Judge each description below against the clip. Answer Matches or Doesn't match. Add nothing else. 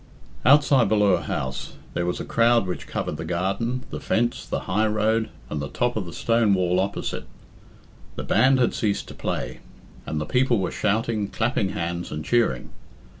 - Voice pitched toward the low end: Matches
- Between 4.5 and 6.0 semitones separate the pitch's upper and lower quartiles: Matches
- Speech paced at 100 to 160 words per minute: Doesn't match